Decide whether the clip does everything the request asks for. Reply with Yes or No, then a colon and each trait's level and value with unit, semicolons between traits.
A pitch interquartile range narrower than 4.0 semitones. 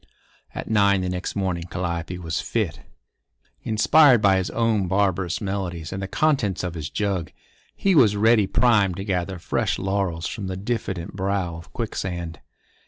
Yes: average, 2.8 semitones